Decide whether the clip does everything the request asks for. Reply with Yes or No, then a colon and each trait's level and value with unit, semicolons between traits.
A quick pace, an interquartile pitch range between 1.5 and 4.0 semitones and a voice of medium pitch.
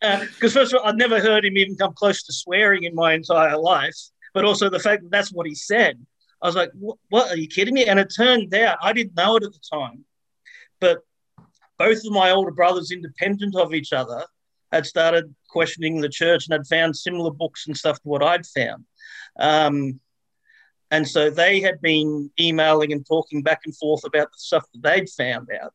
No: fast, 215 wpm; average, 4.6 semitones; medium, 175 Hz